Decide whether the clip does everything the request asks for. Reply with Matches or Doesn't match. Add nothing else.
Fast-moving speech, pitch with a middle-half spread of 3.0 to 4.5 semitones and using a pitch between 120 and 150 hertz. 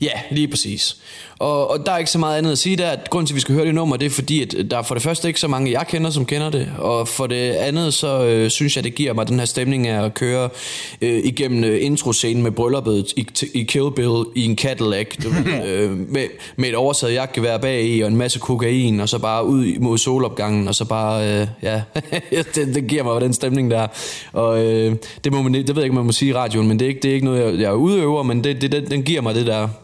Matches